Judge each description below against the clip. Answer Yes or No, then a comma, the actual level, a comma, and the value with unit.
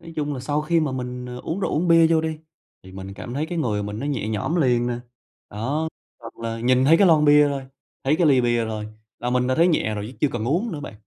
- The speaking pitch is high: No, low, 135 Hz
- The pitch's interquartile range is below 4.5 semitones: No, average, 5.0 semitones